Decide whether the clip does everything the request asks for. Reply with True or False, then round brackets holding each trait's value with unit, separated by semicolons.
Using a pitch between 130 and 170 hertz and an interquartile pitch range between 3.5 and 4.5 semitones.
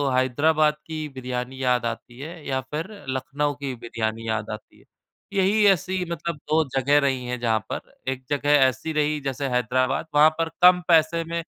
True (140 Hz; 4.2 semitones)